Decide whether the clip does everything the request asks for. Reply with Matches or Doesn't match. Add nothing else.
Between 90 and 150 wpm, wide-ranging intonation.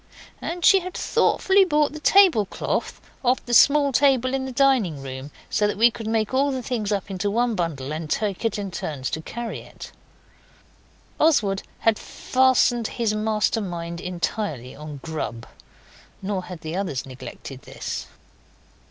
Doesn't match